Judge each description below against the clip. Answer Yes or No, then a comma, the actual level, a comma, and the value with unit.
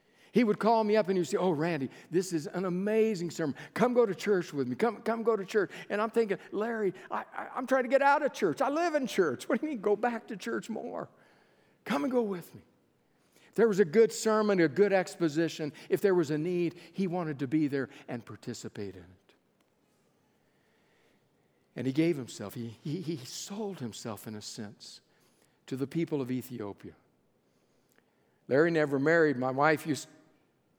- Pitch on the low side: No, medium, 175 Hz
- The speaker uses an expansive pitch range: Yes, wide, 7.0 semitones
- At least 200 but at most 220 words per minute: Yes, fast, 205 wpm